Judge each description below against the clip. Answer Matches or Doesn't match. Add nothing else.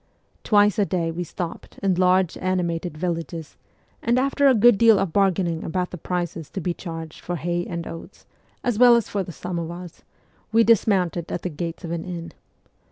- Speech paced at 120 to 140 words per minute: Doesn't match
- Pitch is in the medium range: Matches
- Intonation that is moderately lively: Matches